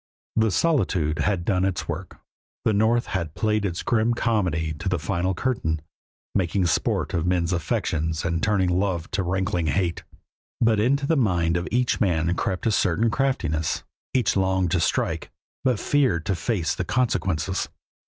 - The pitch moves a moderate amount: Yes, average, 4.6 semitones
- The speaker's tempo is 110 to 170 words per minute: Yes, average, 165 wpm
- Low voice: Yes, very low, 95 Hz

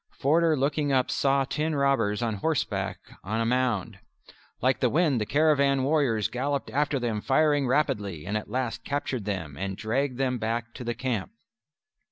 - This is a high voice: No, low, 130 Hz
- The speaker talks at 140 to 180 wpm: Yes, average, 170 wpm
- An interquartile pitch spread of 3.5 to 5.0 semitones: Yes, average, 4.2 semitones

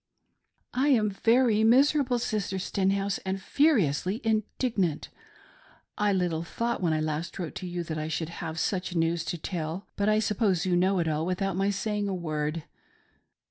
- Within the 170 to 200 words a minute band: Yes, average, 175 wpm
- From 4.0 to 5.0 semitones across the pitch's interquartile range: Yes, average, 4.3 semitones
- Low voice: No, high, 190 Hz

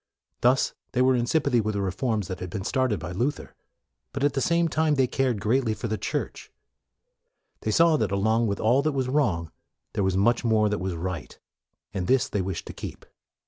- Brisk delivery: Yes, fast, 210 wpm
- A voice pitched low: Yes, low, 115 Hz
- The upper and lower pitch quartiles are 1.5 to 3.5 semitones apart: No, average, 5.2 semitones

